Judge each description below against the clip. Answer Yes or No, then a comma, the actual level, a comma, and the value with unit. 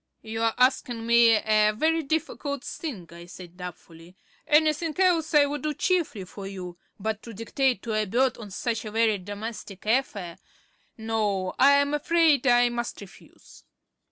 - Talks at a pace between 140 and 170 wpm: Yes, average, 155 wpm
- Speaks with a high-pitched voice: Yes, high, 230 Hz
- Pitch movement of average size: No, wide, 5.8 semitones